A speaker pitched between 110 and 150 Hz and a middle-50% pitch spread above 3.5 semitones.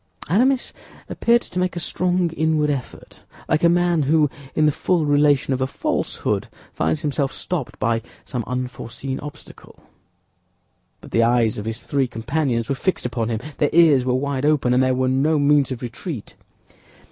Yes: medium, 140 Hz; average, 4.2 semitones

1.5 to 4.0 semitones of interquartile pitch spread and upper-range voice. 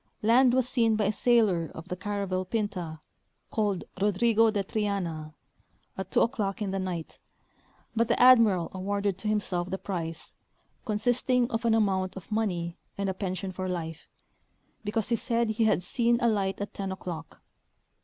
Yes: average, 3.3 semitones; high, 200 Hz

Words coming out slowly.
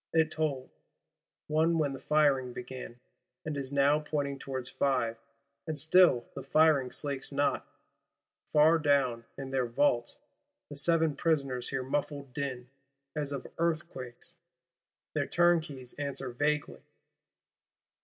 Yes: slow, 120 wpm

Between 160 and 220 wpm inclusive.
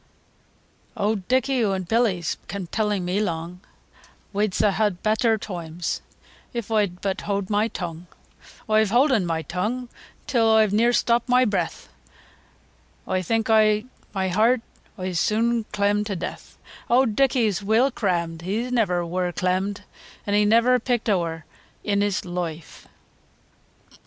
No: average, 140 wpm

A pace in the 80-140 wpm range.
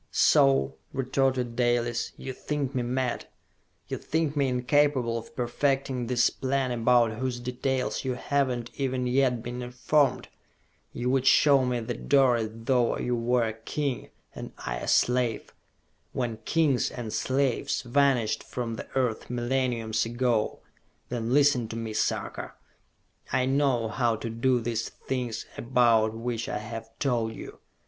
No: average, 150 wpm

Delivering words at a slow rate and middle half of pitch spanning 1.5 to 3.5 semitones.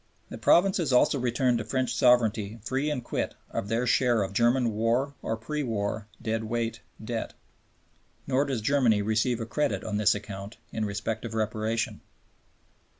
No: average, 160 wpm; average, 2.7 semitones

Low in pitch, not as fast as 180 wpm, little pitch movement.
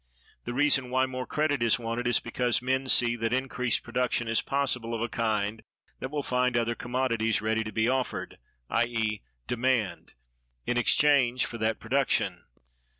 Yes: low, 120 Hz; average, 160 wpm; narrow, 2.3 semitones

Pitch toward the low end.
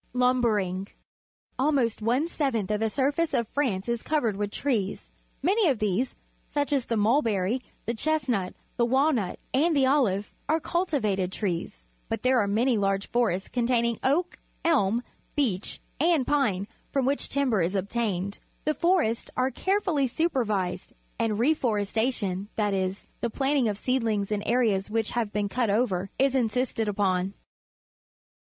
No: high, 235 Hz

